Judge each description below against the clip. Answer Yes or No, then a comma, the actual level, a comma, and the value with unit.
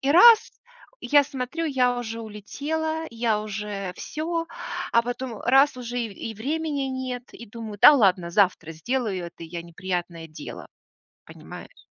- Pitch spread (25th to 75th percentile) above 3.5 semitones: Yes, wide, 5.6 semitones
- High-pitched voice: Yes, high, 235 Hz